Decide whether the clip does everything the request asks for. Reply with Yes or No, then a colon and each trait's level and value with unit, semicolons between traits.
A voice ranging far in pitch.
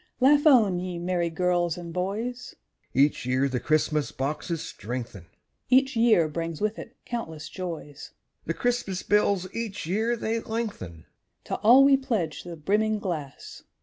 Yes: wide, 6.5 semitones